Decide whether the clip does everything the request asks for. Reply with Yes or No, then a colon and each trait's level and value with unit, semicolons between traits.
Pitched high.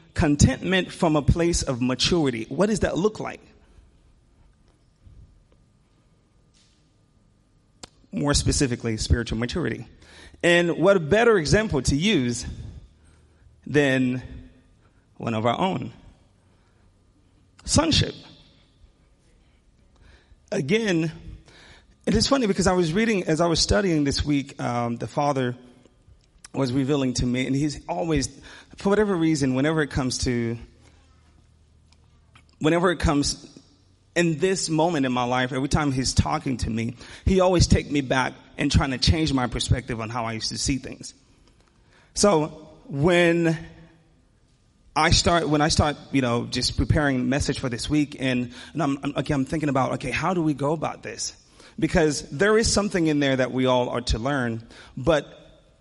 No: low, 135 Hz